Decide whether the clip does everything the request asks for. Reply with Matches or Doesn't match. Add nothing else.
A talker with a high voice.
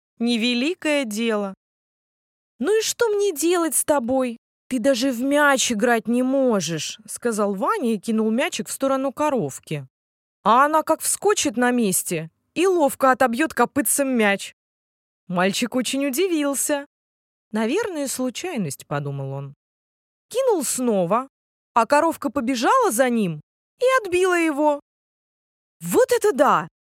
Matches